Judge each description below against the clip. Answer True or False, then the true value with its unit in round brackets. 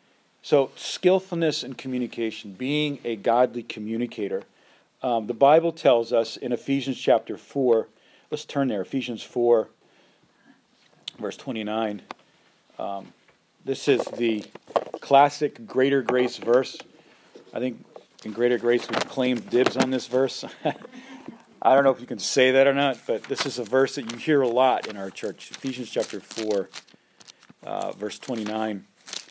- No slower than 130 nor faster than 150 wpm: True (145 wpm)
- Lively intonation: False (2.8 semitones)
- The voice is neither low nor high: False (125 Hz)